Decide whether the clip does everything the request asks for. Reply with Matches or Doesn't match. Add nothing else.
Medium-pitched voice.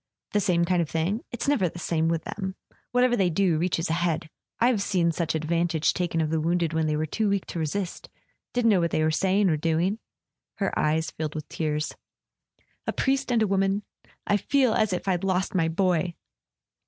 Matches